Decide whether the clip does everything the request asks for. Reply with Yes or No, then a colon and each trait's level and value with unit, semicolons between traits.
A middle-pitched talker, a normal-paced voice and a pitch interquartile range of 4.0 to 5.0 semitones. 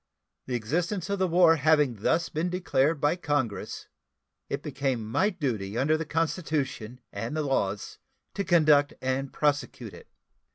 Yes: medium, 150 Hz; average, 150 wpm; average, 4.3 semitones